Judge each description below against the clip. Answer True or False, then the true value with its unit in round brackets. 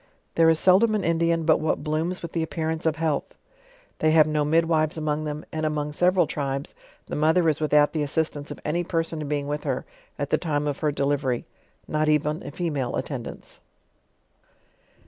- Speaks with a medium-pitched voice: True (155 Hz)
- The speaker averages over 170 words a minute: True (190 wpm)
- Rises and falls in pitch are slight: True (1.7 semitones)